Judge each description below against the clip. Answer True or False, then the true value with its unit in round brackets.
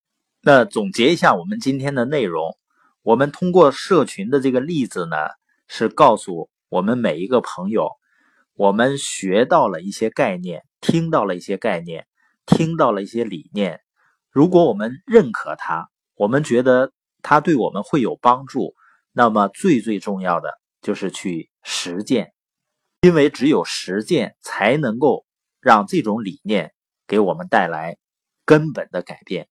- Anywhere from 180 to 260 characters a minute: True (230 characters per minute)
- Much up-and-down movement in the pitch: True (7.0 semitones)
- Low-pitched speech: True (130 Hz)